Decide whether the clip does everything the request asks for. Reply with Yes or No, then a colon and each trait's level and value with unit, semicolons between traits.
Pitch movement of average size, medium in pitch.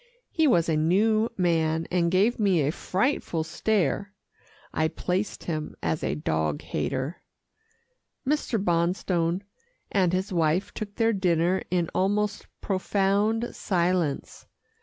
Yes: average, 3.8 semitones; medium, 180 Hz